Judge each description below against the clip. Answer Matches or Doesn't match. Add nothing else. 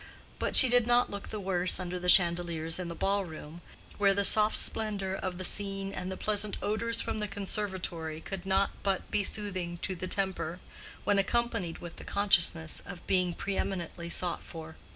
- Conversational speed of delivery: Matches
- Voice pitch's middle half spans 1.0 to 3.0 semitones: Matches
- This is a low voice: Doesn't match